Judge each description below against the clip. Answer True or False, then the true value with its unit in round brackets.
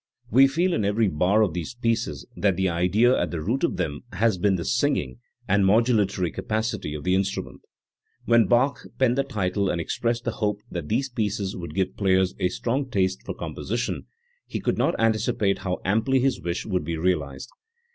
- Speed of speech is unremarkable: True (190 wpm)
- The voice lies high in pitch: False (100 Hz)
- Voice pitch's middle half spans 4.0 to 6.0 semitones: True (4.3 semitones)